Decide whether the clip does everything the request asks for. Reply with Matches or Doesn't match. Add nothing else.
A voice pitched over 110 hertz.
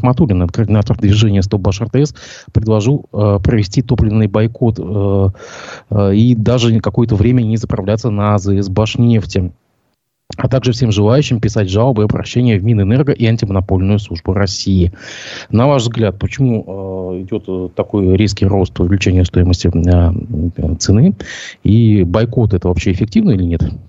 Doesn't match